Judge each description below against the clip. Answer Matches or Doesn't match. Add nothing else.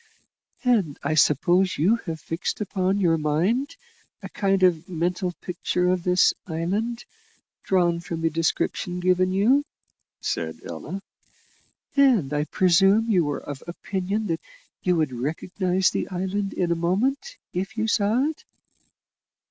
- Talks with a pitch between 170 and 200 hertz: Matches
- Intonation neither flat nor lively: Matches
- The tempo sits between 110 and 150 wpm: Matches